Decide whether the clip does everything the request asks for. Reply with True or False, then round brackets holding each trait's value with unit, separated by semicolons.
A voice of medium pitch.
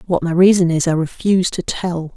True (175 Hz)